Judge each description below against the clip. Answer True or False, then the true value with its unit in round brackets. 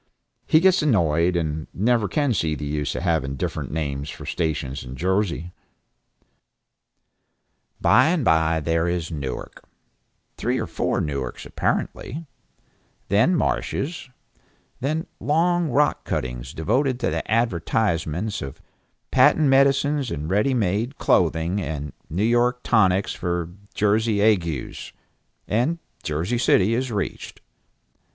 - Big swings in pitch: True (7.6 semitones)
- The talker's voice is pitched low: True (95 Hz)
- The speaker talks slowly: True (120 wpm)